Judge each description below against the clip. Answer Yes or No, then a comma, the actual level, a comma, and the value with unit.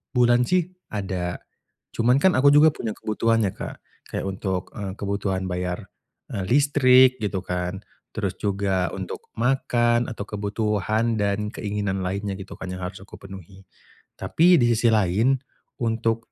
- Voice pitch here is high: No, low, 105 Hz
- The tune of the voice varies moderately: Yes, average, 3.6 semitones